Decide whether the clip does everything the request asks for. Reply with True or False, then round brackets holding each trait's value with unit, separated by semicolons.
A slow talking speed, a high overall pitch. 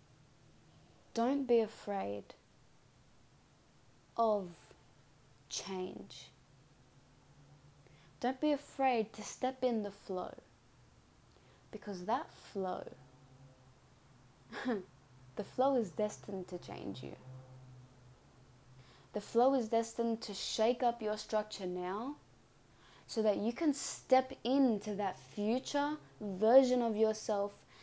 True (95 wpm; 205 Hz)